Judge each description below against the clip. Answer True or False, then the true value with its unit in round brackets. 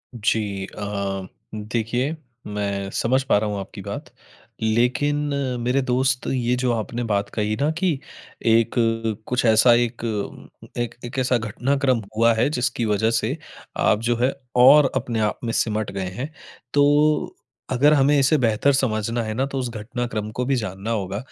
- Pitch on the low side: True (120 Hz)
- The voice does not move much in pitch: False (3.2 semitones)